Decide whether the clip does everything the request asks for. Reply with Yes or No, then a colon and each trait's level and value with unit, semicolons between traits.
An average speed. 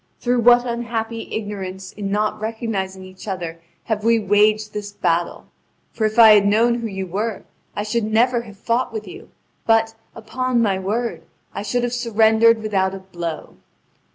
Yes: average, 170 wpm